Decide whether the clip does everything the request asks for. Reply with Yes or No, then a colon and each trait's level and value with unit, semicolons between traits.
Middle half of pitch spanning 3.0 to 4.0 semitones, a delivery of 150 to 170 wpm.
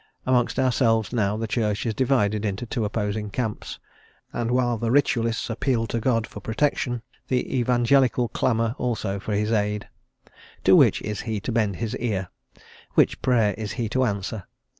No: narrow, 2.5 semitones; average, 165 wpm